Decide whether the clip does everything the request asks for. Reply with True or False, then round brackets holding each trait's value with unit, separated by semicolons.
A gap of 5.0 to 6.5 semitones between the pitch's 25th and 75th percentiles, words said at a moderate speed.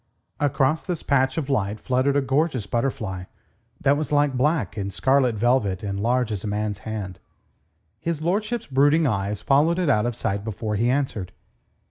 True (5.4 semitones; 170 wpm)